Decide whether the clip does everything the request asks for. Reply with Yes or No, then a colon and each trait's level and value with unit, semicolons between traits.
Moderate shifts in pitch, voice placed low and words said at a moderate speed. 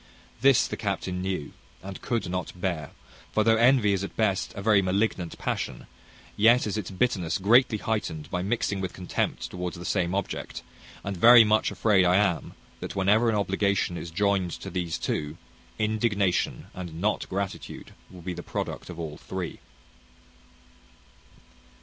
Yes: average, 3.1 semitones; very low, 95 Hz; average, 160 wpm